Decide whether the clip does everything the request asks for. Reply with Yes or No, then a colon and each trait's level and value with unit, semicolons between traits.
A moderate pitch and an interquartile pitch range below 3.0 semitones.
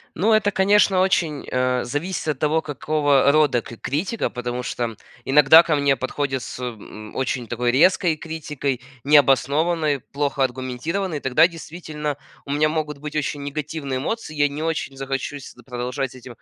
No: medium, 145 Hz; average, 3.4 semitones